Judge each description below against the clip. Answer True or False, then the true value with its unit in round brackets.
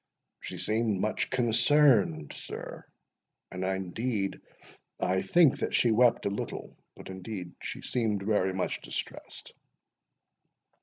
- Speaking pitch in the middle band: False (105 Hz)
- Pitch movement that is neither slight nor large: True (3.9 semitones)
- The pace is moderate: False (110 wpm)